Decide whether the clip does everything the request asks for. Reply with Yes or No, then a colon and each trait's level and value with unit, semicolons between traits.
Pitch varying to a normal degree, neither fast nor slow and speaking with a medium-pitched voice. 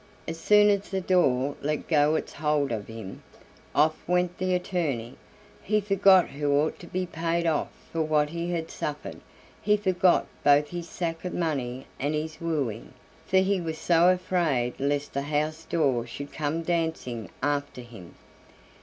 Yes: average, 3.7 semitones; average, 165 wpm; medium, 160 Hz